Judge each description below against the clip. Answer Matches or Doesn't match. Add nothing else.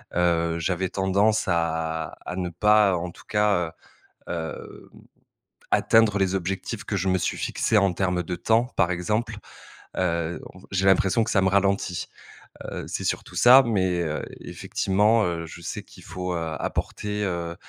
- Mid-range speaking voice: Doesn't match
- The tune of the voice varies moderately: Matches